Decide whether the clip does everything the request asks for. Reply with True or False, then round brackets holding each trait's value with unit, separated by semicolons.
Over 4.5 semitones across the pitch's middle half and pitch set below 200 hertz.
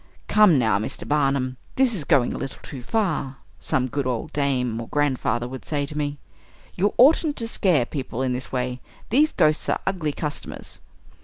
True (5.2 semitones; 140 Hz)